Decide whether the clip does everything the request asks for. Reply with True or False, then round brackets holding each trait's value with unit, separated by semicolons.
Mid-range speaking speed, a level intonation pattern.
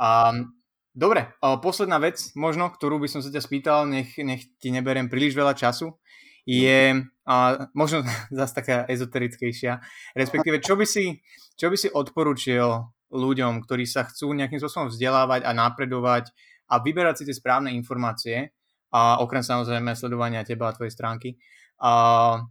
False (150 wpm; 3.2 semitones)